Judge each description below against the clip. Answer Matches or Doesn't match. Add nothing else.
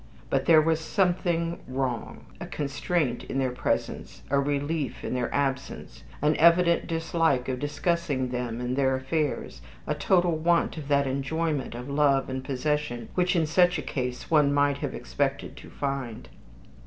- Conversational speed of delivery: Matches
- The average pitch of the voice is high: Doesn't match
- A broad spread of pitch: Doesn't match